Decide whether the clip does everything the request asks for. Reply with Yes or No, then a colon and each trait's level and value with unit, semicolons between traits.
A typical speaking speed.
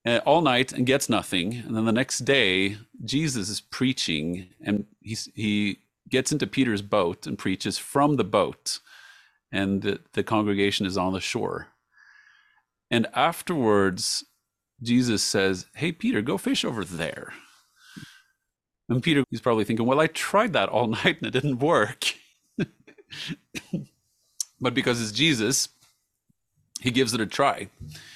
Yes: average, 145 wpm